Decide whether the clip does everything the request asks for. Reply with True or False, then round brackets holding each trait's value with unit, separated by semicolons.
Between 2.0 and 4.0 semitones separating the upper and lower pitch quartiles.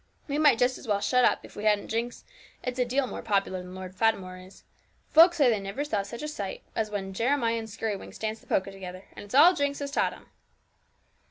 False (4.8 semitones)